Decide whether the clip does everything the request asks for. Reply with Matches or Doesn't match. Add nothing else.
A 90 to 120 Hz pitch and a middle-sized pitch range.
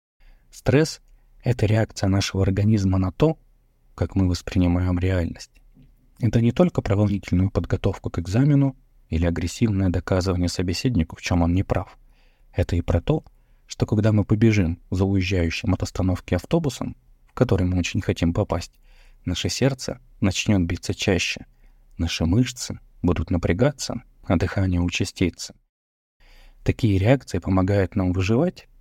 Matches